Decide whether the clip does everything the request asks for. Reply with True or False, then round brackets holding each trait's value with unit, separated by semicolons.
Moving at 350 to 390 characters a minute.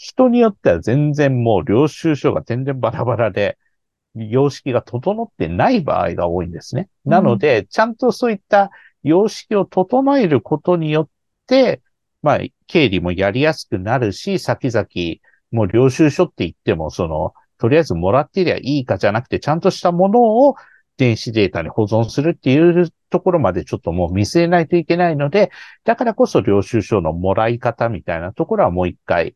True (370 characters per minute)